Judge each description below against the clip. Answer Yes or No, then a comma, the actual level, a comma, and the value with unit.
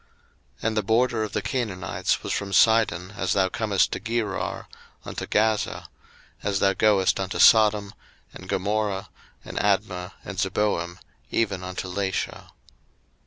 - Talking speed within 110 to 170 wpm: Yes, average, 140 wpm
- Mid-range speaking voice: No, low, 100 Hz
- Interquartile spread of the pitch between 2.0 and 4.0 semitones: Yes, narrow, 2.4 semitones